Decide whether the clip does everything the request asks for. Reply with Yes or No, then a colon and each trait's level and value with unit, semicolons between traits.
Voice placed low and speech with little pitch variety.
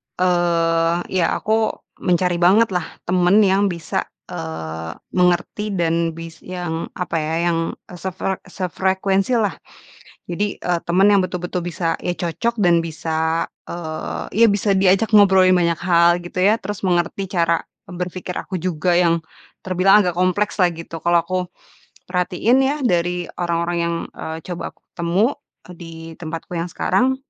No: medium, 175 Hz; narrow, 2.1 semitones